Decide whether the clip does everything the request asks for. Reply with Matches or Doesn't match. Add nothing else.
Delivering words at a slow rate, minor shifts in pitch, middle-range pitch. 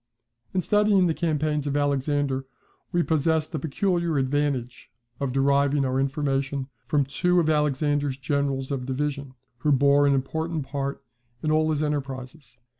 Doesn't match